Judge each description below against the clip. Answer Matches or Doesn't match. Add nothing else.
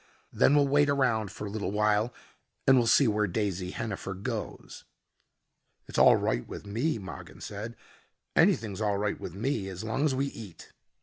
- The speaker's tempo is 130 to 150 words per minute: Doesn't match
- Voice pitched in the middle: Doesn't match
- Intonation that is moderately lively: Matches